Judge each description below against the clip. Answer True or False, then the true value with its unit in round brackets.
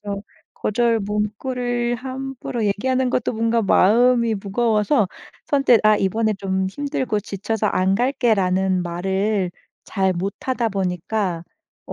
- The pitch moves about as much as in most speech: True (3.9 semitones)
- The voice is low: False (215 Hz)